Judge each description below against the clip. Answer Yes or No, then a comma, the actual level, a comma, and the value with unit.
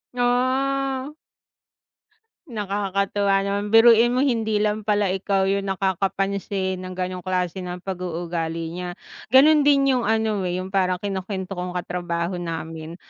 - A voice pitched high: Yes, high, 195 Hz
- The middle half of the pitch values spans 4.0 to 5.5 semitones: No, average, 3.4 semitones